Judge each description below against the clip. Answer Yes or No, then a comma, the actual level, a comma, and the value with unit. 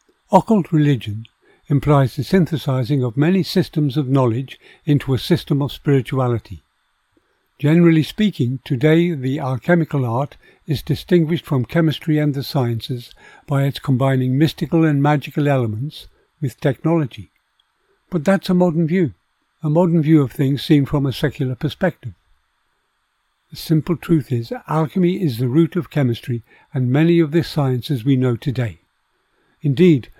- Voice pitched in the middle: Yes, medium, 145 Hz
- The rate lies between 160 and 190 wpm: No, average, 140 wpm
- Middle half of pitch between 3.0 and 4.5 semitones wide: Yes, average, 4.1 semitones